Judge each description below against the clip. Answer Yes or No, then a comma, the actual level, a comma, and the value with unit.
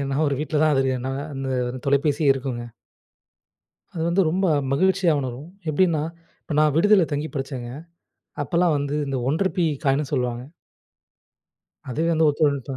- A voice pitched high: No, medium, 145 Hz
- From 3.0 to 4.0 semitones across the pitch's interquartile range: Yes, average, 3.4 semitones